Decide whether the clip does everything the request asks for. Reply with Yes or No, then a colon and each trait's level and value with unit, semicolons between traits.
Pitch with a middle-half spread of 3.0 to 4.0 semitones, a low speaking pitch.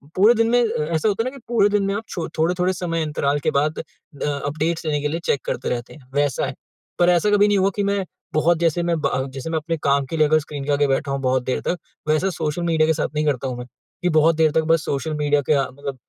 No: average, 3.5 semitones; medium, 155 Hz